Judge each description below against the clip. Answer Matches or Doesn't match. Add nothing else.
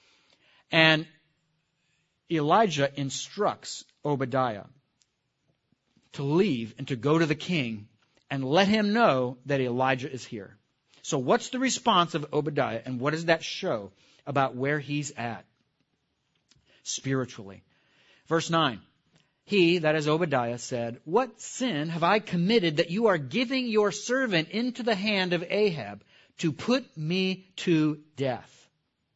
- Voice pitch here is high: Doesn't match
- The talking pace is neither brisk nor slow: Doesn't match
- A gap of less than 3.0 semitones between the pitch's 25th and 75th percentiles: Doesn't match